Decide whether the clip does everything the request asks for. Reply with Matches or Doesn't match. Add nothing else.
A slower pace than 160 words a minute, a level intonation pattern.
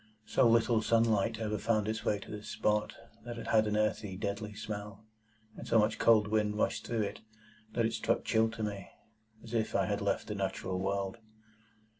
Doesn't match